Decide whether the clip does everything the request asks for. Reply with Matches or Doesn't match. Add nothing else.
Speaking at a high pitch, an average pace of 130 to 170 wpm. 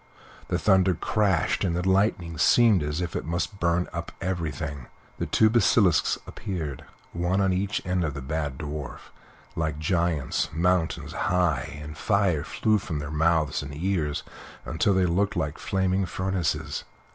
Doesn't match